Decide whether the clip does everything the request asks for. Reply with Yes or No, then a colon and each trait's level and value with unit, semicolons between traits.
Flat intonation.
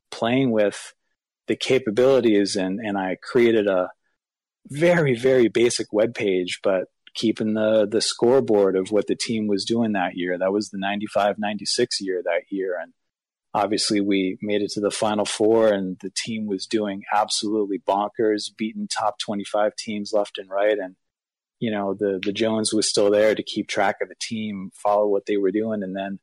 Yes: narrow, 1.8 semitones